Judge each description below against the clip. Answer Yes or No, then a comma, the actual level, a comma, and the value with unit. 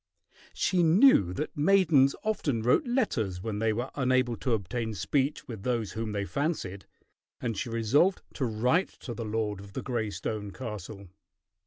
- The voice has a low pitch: Yes, low, 115 Hz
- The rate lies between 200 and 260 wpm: No, average, 165 wpm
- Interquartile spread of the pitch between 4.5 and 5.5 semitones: Yes, average, 5.1 semitones